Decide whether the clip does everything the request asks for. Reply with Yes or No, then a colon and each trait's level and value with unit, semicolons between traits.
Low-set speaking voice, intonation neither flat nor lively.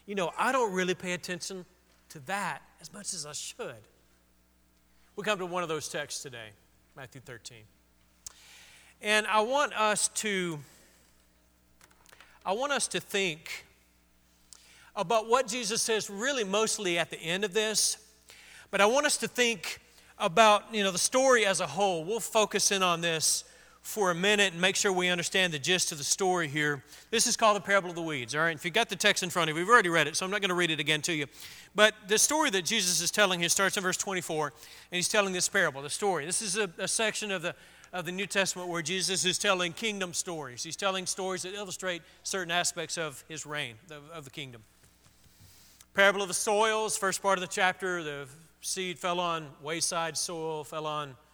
No: medium, 180 Hz; average, 4.6 semitones